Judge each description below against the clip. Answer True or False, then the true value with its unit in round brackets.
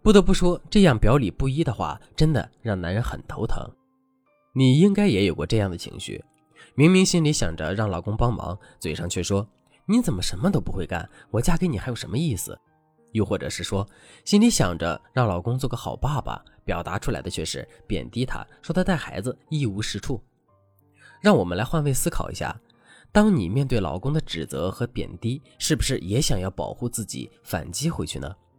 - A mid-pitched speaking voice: False (125 Hz)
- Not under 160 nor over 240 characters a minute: False (290 characters per minute)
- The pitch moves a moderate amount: False (8.2 semitones)